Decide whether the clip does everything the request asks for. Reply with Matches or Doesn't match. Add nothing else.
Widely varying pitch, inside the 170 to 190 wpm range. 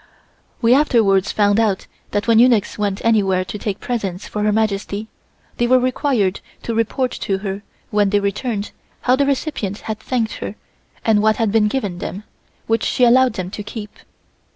Doesn't match